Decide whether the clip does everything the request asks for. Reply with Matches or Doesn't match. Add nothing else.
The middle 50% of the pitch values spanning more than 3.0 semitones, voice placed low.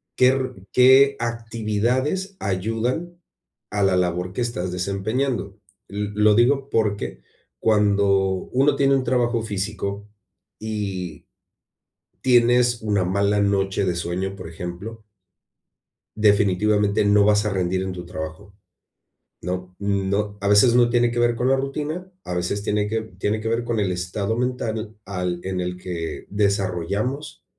Matches